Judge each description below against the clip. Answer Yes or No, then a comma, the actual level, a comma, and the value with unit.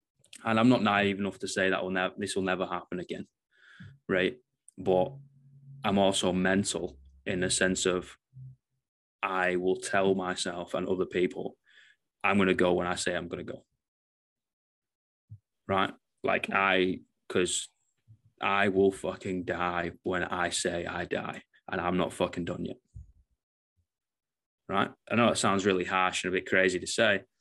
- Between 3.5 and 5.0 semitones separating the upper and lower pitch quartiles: No, average, 2.9 semitones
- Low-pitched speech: Yes, very low, 95 Hz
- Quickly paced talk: No, average, 160 wpm